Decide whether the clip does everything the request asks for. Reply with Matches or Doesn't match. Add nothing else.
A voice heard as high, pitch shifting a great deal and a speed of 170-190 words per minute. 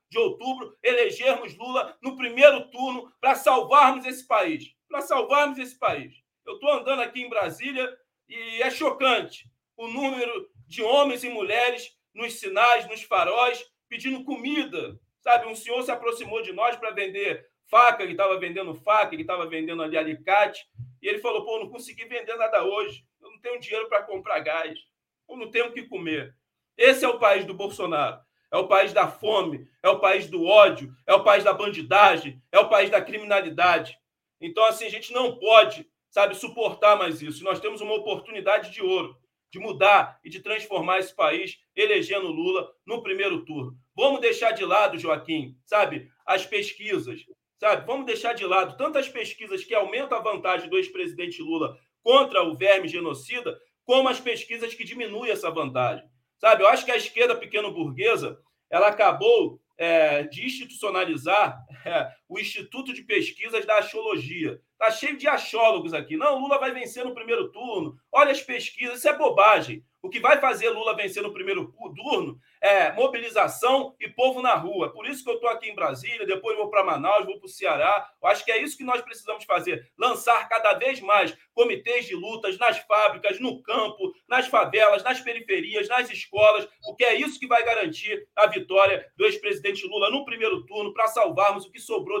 Matches